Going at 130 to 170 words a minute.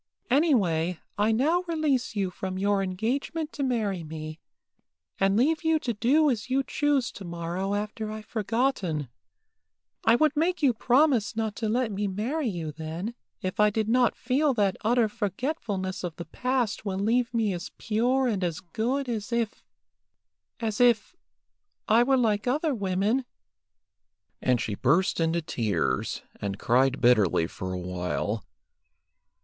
Yes: average, 155 wpm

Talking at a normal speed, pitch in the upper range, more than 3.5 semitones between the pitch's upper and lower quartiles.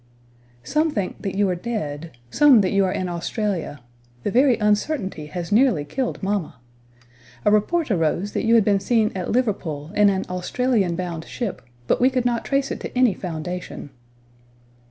Yes: average, 175 wpm; high, 205 Hz; average, 5.2 semitones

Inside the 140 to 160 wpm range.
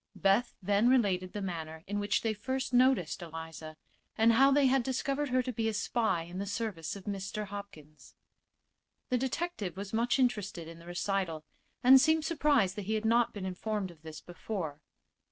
No: average, 185 wpm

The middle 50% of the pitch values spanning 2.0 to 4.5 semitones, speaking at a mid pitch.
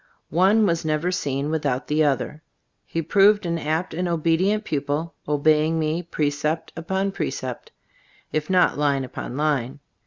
Yes: average, 3.0 semitones; medium, 155 Hz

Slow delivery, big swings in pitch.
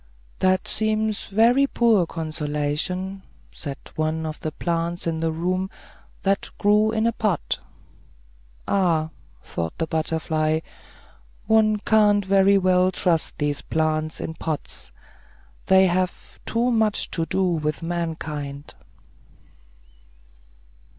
No: slow, 110 wpm; average, 4.2 semitones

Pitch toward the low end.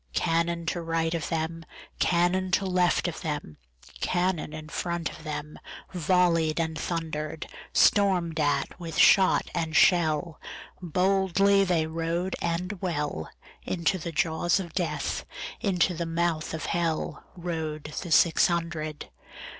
No: medium, 170 Hz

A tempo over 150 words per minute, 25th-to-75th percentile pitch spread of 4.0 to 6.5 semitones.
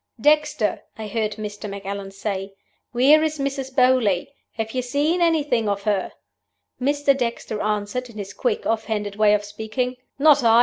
Yes: average, 165 wpm; average, 4.9 semitones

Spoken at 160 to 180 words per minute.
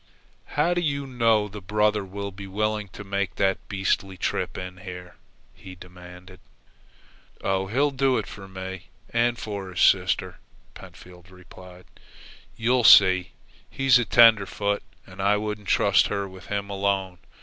No: average, 145 wpm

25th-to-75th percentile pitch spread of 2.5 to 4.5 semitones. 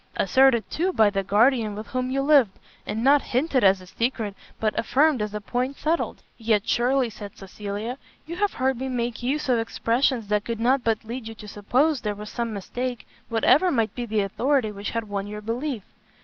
Yes: average, 3.9 semitones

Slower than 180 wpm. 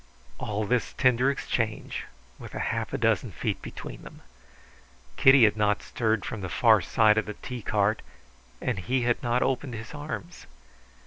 Yes: average, 165 wpm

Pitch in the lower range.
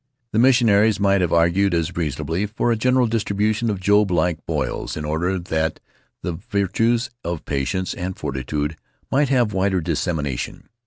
Yes: very low, 95 Hz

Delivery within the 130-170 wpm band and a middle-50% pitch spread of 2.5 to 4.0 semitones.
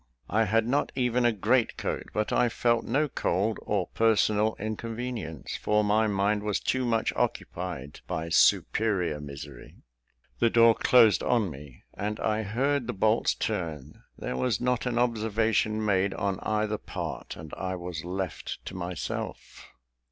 Yes: average, 150 wpm; average, 3.7 semitones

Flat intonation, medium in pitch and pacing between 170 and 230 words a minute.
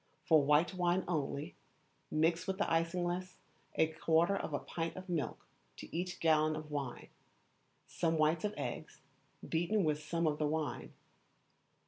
No: narrow, 2.3 semitones; medium, 165 Hz; average, 150 wpm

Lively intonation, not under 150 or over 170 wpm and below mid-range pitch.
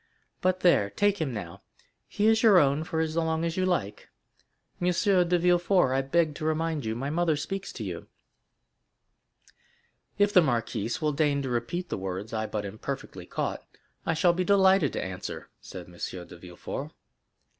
No: wide, 8.1 semitones; average, 165 wpm; medium, 155 Hz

